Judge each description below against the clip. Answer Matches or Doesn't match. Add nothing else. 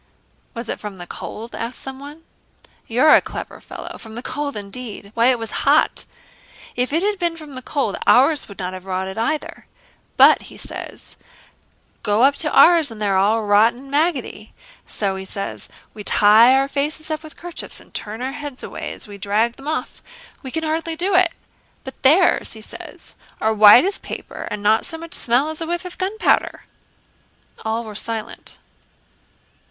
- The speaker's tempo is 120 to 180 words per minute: Doesn't match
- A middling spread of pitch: Doesn't match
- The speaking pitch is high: Matches